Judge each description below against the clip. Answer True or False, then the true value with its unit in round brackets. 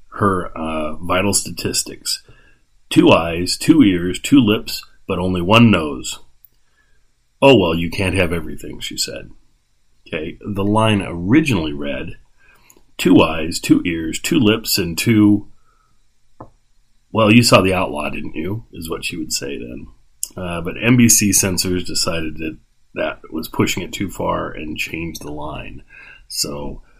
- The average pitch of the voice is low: True (95 Hz)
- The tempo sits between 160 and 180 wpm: False (145 wpm)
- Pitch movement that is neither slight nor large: True (5.0 semitones)